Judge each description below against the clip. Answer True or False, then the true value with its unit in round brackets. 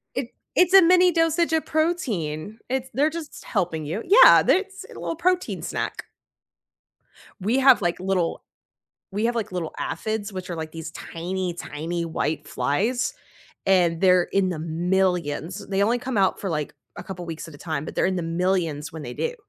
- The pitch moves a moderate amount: False (7.9 semitones)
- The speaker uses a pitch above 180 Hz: True (190 Hz)